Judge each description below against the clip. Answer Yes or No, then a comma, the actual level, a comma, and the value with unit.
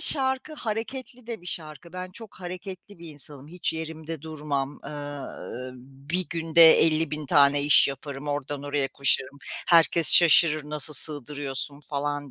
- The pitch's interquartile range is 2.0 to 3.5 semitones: Yes, average, 3.2 semitones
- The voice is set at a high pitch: No, medium, 150 Hz